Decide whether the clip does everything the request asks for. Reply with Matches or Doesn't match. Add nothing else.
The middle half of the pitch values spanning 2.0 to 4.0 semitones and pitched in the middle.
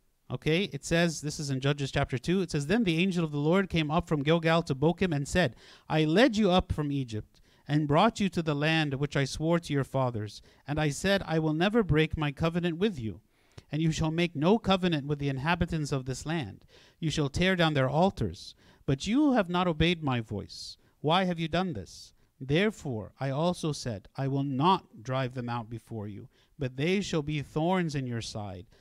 Doesn't match